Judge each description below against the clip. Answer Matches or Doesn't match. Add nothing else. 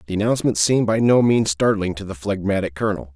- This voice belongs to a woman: Doesn't match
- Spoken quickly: Matches